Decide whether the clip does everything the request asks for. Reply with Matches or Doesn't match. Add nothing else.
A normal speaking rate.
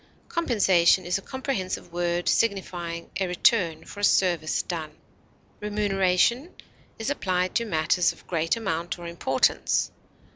Doesn't match